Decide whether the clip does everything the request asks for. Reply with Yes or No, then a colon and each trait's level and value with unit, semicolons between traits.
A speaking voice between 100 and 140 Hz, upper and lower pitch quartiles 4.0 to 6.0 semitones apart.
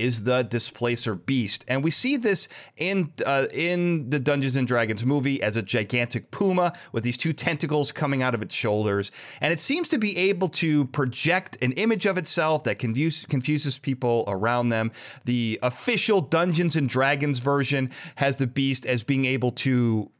Yes: low, 135 Hz; average, 5.1 semitones